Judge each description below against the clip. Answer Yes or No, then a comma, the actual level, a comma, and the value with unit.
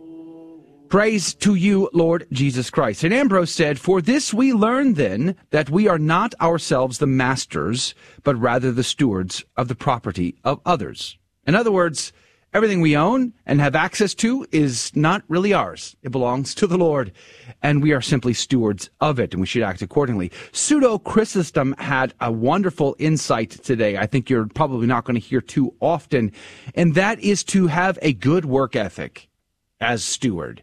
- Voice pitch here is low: No, medium, 150 Hz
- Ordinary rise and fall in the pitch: No, wide, 6.3 semitones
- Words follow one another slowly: No, average, 175 wpm